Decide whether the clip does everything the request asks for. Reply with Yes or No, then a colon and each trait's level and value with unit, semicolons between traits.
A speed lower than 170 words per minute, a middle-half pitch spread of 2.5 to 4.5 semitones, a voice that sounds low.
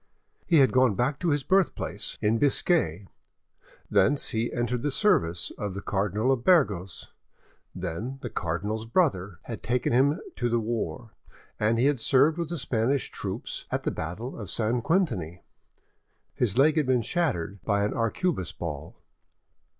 No: average, 155 wpm; wide, 5.5 semitones; low, 120 Hz